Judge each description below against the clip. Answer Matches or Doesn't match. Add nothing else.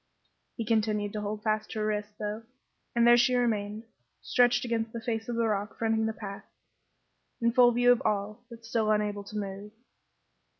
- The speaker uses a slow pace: Doesn't match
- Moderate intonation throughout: Doesn't match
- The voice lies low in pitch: Doesn't match